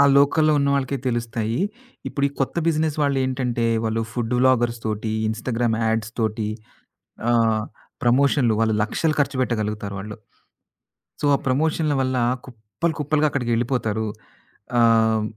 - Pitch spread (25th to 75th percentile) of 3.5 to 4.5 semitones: Yes, average, 3.8 semitones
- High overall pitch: No, low, 120 Hz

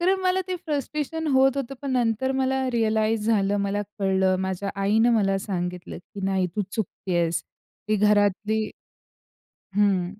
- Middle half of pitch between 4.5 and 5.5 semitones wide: Yes, average, 5.2 semitones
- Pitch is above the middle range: Yes, high, 210 Hz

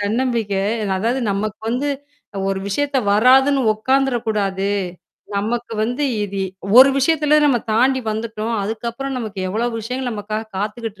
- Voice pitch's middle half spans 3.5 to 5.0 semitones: Yes, average, 3.8 semitones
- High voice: Yes, high, 230 Hz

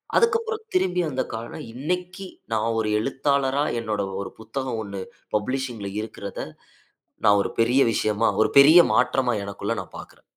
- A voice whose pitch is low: Yes, low, 130 Hz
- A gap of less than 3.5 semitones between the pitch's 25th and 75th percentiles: No, average, 5.1 semitones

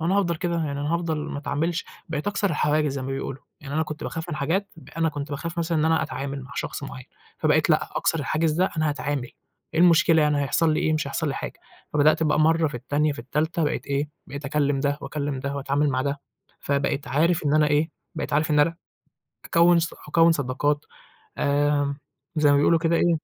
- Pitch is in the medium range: Yes, medium, 150 Hz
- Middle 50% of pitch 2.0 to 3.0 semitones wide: Yes, narrow, 2.4 semitones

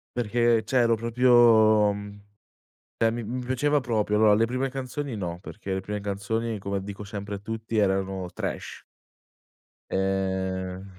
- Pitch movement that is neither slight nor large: Yes, average, 3.3 semitones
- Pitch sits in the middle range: No, low, 105 Hz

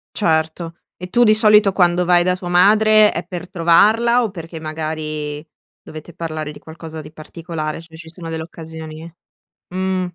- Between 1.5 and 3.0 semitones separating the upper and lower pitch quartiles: Yes, average, 2.7 semitones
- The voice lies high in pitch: No, medium, 170 Hz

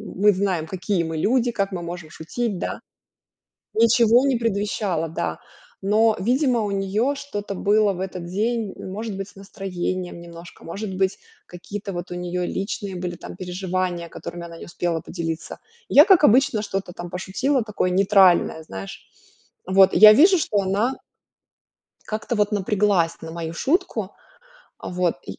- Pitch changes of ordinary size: Yes, average, 3.5 semitones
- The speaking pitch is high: Yes, high, 195 Hz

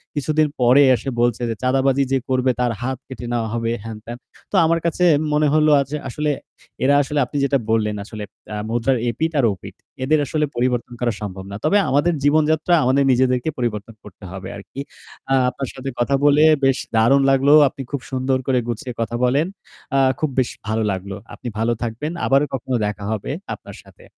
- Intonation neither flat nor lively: Yes, average, 3.8 semitones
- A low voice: Yes, low, 130 Hz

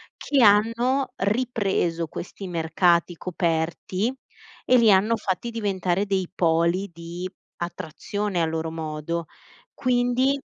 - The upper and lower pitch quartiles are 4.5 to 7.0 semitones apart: Yes, average, 5.1 semitones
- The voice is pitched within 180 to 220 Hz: Yes, high, 190 Hz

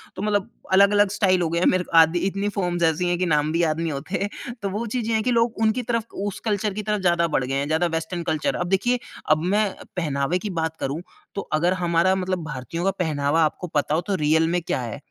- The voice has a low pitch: No, medium, 175 Hz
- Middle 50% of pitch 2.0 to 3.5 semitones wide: No, average, 4.0 semitones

